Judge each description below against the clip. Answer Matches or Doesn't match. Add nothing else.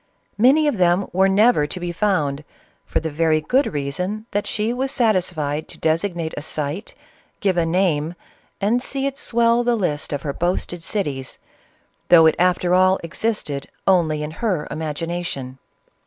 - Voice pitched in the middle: Matches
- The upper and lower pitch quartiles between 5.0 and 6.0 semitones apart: Matches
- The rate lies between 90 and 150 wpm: Doesn't match